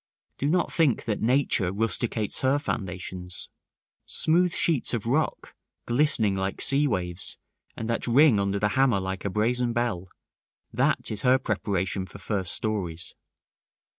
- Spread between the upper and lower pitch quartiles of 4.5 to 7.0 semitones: Yes, wide, 5.4 semitones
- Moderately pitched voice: No, low, 110 Hz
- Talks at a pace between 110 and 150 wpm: Yes, average, 140 wpm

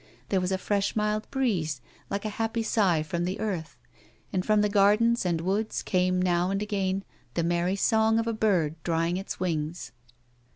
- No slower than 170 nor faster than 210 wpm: Yes, average, 180 wpm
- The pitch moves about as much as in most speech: Yes, average, 3.5 semitones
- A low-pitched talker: No, high, 190 Hz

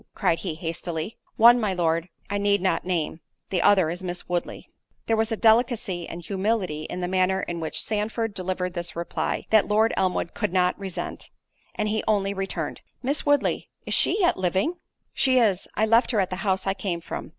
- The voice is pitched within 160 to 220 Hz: Yes, high, 190 Hz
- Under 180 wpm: No, average, 185 wpm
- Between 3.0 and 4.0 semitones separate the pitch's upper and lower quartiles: Yes, average, 3.7 semitones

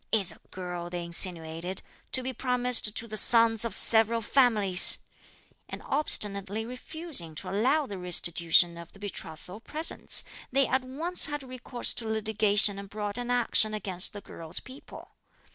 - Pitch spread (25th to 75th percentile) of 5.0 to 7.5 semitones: Yes, average, 5.3 semitones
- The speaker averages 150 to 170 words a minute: Yes, average, 155 wpm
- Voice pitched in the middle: No, high, 215 Hz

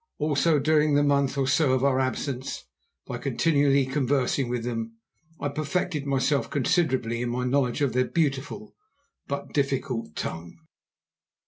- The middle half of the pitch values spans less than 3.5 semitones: Yes, narrow, 2.4 semitones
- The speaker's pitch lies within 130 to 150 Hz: Yes, medium, 140 Hz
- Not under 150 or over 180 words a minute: No, average, 140 wpm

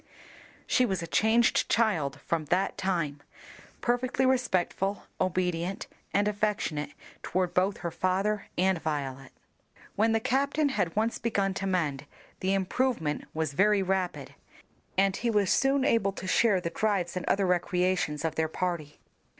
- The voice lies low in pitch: No, high, 190 Hz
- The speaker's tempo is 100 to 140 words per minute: No, average, 150 wpm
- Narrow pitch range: No, average, 4.0 semitones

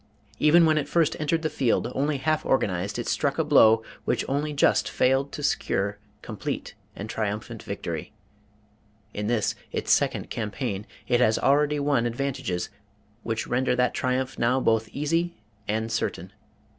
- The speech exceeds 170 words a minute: No, average, 155 wpm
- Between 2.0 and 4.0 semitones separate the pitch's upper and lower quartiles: No, average, 4.9 semitones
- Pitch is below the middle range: Yes, low, 130 Hz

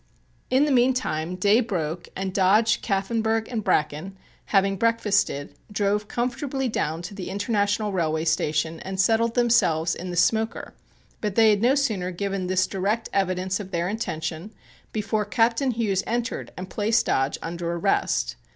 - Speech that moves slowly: No, average, 150 wpm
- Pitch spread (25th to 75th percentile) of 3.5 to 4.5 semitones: Yes, average, 4.0 semitones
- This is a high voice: Yes, high, 200 Hz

